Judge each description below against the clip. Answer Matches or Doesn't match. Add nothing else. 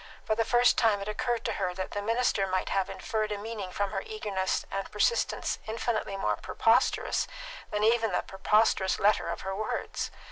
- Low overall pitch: Doesn't match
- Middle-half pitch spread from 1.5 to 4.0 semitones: Matches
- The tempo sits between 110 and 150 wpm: Doesn't match